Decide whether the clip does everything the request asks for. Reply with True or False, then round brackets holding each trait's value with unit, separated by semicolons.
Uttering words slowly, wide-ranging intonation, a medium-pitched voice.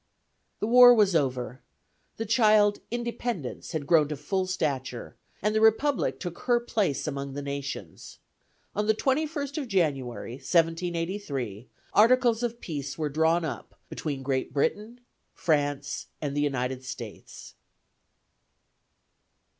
True (125 wpm; 7.9 semitones; 165 Hz)